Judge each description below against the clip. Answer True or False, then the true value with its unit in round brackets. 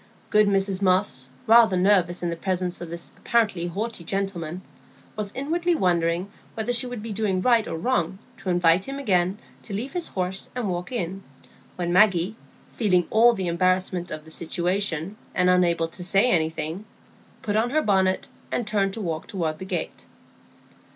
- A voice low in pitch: False (190 Hz)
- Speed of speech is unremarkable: True (170 wpm)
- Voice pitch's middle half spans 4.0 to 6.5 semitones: False (3.5 semitones)